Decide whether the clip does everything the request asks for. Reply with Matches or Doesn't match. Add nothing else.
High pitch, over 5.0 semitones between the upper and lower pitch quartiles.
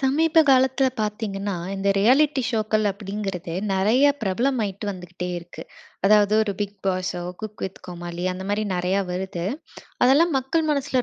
Matches